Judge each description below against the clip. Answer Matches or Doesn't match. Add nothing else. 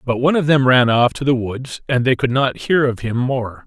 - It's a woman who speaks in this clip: Doesn't match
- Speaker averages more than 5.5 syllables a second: Doesn't match